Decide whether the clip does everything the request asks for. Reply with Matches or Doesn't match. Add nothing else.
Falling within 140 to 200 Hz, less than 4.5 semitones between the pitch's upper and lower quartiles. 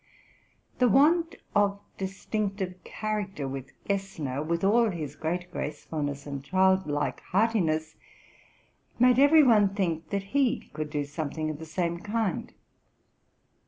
Doesn't match